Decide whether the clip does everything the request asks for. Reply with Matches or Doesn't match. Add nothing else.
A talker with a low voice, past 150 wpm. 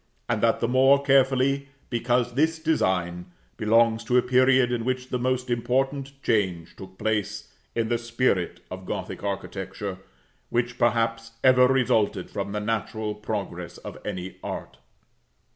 Doesn't match